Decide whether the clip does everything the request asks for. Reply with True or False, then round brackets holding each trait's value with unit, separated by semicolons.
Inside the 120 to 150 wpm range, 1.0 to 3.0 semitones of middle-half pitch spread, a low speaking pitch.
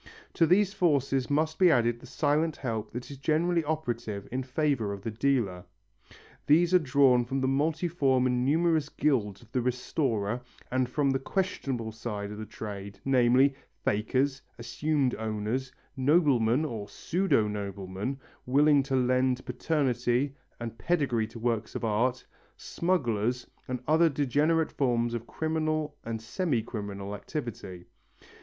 False (140 wpm; 4.7 semitones; 130 Hz)